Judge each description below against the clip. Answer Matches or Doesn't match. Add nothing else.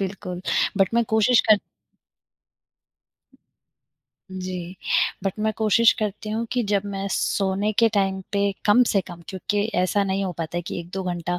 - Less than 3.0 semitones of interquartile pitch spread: Matches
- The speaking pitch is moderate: Doesn't match